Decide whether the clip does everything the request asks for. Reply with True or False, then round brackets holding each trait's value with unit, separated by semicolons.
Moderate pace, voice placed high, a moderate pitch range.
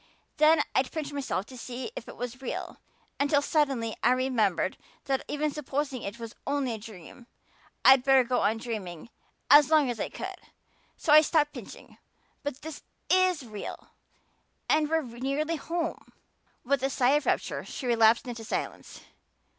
True (160 wpm; 265 Hz; 3.9 semitones)